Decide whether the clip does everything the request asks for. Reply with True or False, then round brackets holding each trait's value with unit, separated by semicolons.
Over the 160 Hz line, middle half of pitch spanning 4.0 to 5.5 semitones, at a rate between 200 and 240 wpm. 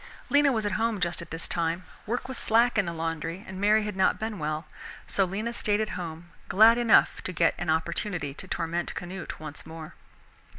True (185 Hz; 4.7 semitones; 205 wpm)